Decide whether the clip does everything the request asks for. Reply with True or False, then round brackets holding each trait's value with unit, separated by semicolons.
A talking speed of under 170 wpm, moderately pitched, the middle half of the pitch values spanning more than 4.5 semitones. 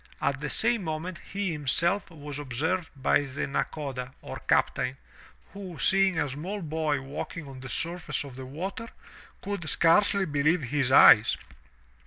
True (150 wpm; 155 Hz; 4.9 semitones)